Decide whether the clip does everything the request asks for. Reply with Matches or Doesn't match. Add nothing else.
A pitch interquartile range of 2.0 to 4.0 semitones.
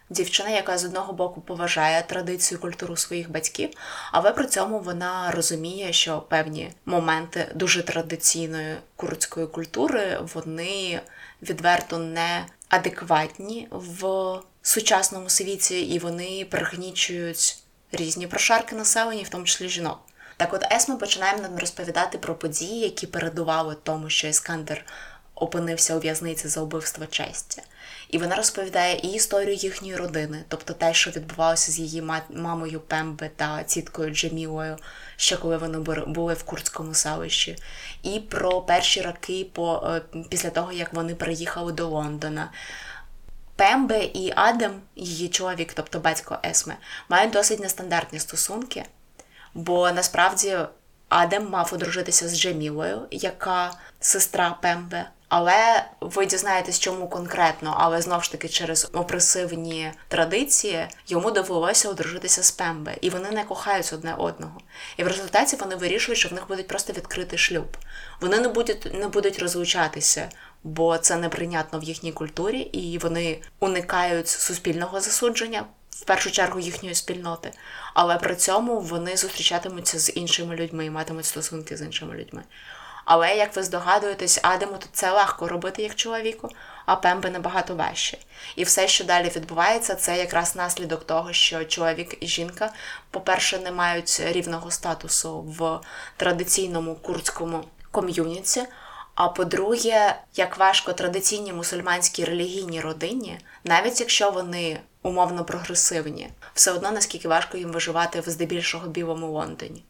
Matches